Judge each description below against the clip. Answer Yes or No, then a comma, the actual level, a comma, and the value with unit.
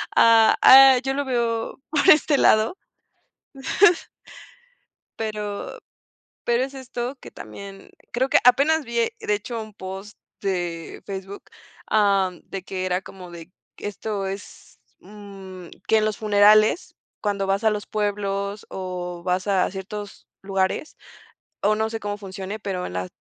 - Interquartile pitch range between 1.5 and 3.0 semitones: Yes, average, 2.7 semitones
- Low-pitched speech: No, high, 205 Hz